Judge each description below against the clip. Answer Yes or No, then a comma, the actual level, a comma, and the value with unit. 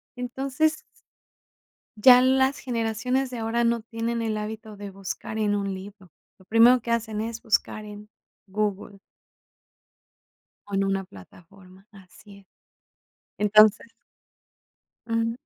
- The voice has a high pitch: Yes, high, 215 Hz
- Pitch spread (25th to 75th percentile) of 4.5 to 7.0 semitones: No, average, 2.8 semitones